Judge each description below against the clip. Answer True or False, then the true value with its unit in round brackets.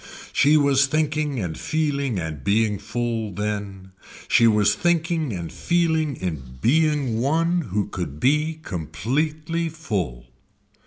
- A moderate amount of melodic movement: False (7.8 semitones)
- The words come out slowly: True (120 wpm)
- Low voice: True (125 Hz)